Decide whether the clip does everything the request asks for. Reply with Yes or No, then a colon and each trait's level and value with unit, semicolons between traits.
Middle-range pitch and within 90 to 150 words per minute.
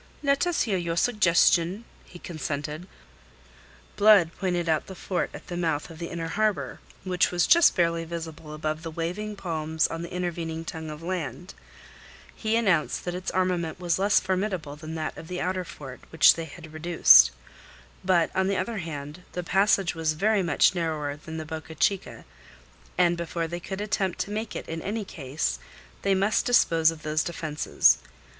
No: medium, 170 Hz; average, 175 wpm